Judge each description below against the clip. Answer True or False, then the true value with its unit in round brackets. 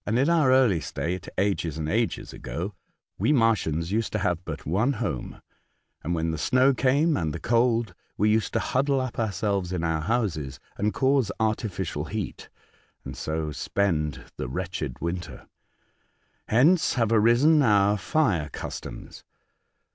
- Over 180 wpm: False (150 wpm)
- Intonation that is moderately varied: False (6.5 semitones)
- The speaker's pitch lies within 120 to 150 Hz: False (105 Hz)